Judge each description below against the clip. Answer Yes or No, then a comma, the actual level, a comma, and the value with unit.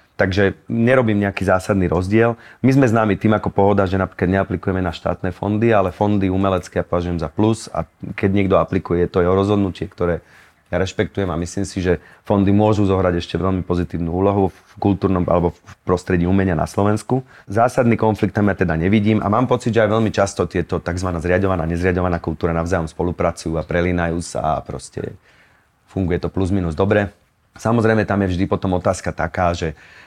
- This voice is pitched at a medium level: No, very low, 95 Hz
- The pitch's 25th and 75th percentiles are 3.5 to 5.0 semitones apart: No, average, 2.8 semitones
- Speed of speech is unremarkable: No, fast, 180 wpm